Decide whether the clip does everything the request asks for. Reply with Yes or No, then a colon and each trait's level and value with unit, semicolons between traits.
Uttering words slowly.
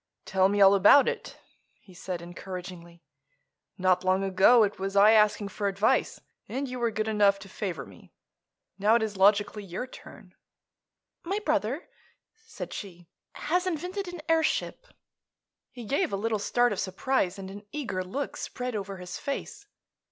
No: average, 160 wpm